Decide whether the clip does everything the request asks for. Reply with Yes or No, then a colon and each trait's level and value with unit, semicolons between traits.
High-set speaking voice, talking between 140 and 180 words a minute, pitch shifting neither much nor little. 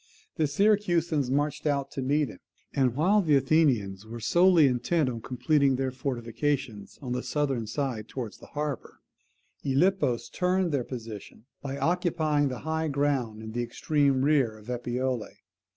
No: low, 135 Hz; average, 150 wpm; average, 4.1 semitones